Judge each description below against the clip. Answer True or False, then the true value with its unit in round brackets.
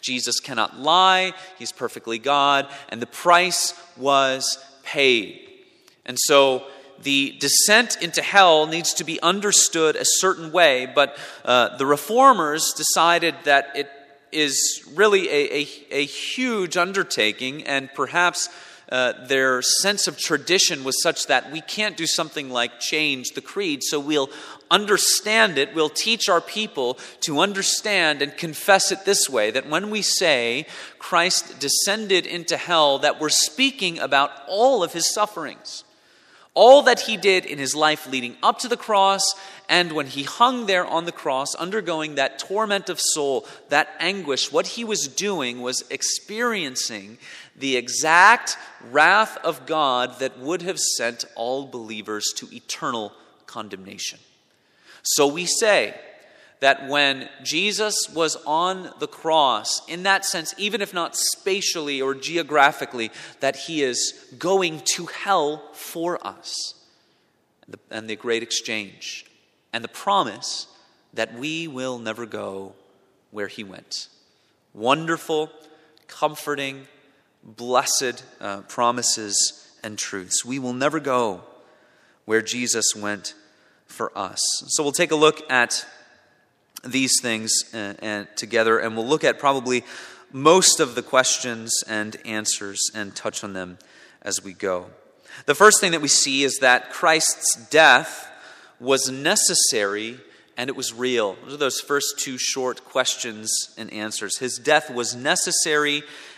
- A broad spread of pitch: True (5.7 semitones)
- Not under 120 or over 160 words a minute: True (140 wpm)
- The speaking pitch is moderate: True (145 Hz)